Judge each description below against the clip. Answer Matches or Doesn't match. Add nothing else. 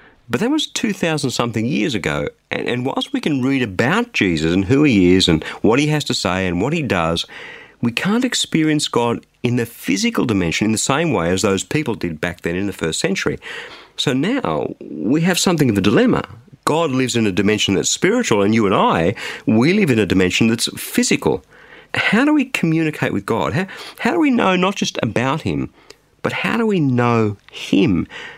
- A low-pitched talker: Matches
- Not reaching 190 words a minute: Doesn't match